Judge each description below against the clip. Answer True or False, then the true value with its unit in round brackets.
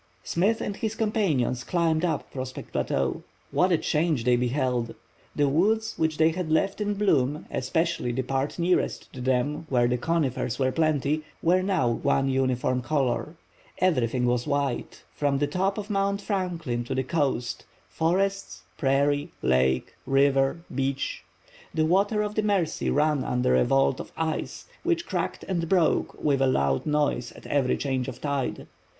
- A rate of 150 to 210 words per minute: True (160 wpm)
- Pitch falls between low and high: True (145 Hz)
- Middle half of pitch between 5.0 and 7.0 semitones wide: True (5.4 semitones)